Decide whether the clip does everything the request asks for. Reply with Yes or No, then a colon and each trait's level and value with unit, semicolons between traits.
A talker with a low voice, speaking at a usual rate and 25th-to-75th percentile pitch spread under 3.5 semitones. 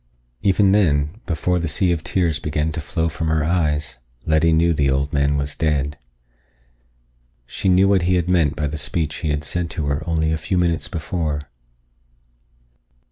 Yes: very low, 80 Hz; average, 180 wpm; average, 2.9 semitones